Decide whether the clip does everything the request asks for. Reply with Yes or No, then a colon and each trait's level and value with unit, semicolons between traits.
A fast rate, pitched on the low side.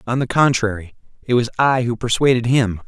No: average, 190 wpm; low, 120 Hz